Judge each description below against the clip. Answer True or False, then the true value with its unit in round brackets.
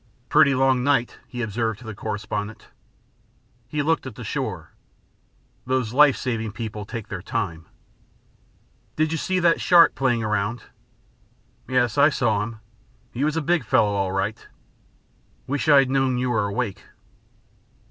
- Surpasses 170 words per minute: False (150 wpm)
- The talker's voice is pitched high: False (120 Hz)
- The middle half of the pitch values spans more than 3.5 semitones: True (4.3 semitones)